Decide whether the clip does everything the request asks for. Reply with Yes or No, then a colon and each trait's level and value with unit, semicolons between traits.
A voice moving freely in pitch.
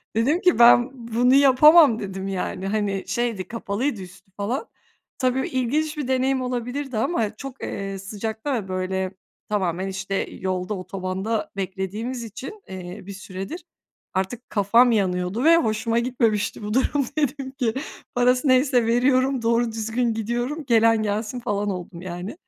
No: average, 4.7 semitones